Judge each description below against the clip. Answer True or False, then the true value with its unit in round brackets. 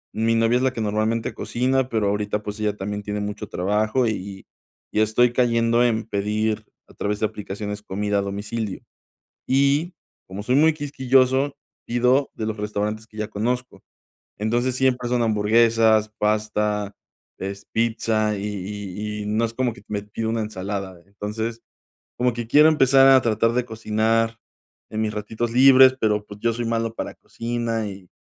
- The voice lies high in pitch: False (110 Hz)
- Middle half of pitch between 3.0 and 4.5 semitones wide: False (2.5 semitones)